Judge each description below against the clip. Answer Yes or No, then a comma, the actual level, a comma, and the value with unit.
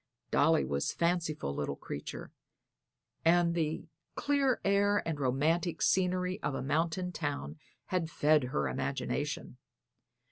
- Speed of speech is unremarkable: No, slow, 120 wpm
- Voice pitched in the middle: Yes, medium, 165 Hz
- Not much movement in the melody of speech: No, average, 4.1 semitones